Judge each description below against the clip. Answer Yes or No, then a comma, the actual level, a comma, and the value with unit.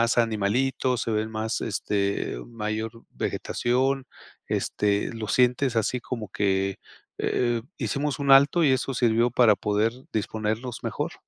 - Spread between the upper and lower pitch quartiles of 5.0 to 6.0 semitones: No, average, 2.9 semitones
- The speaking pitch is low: Yes, low, 115 Hz